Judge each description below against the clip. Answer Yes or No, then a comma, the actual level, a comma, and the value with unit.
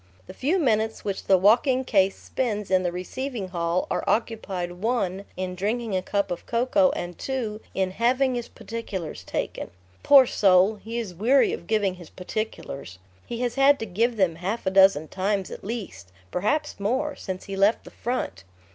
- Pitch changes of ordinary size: Yes, average, 4.5 semitones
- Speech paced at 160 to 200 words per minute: Yes, average, 180 wpm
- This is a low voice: No, high, 210 Hz